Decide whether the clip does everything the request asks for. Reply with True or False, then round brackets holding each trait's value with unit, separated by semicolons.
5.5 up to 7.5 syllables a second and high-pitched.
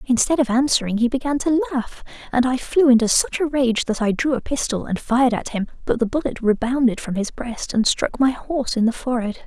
True (5.7 syllables/s; 245 Hz)